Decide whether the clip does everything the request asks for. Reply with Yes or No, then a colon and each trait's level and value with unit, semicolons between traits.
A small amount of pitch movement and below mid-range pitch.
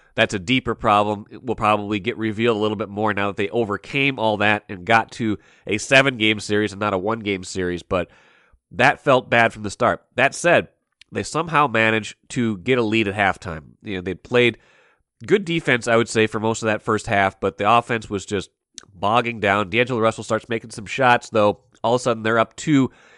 Yes: narrow, 2.3 semitones; low, 110 Hz